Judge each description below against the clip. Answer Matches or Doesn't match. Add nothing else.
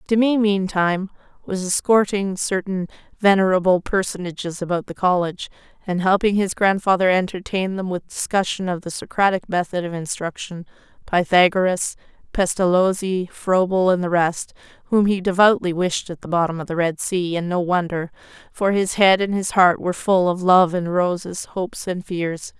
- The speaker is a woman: Matches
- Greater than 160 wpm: Doesn't match